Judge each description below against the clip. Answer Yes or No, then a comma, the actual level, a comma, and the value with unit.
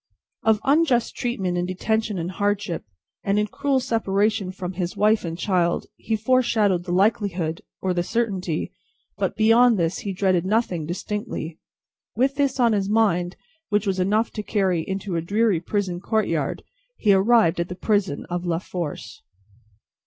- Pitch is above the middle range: Yes, high, 195 Hz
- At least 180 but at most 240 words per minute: No, average, 160 wpm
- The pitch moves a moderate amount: Yes, average, 3.7 semitones